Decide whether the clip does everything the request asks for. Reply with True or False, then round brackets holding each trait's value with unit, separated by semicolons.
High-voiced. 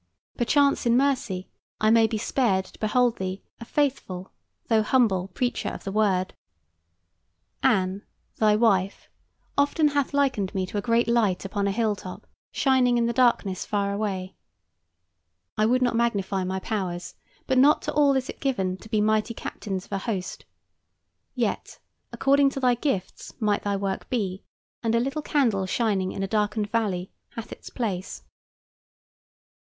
True (215 Hz)